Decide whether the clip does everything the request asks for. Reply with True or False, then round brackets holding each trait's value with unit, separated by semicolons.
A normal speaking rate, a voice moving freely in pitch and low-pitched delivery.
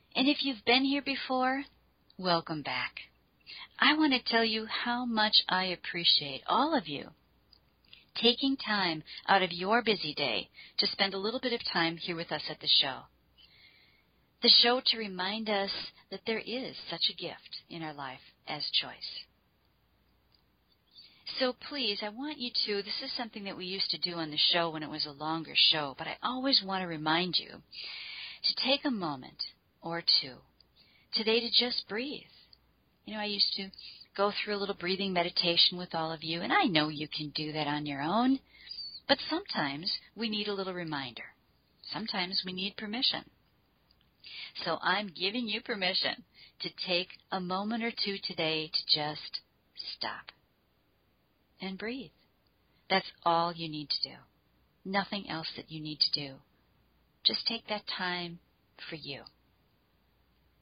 False (165 wpm; 5.9 semitones; 190 Hz)